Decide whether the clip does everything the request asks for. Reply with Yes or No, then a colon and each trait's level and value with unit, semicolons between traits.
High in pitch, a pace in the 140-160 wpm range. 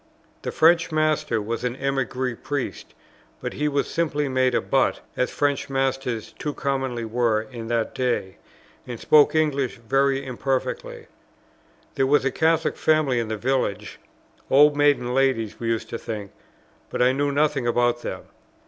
No: low, 130 Hz; average, 155 wpm